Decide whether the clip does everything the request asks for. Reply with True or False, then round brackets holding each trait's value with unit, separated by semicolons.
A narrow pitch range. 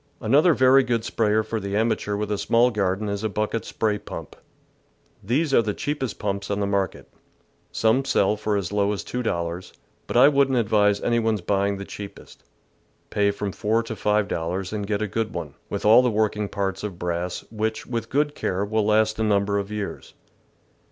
True (2.2 semitones)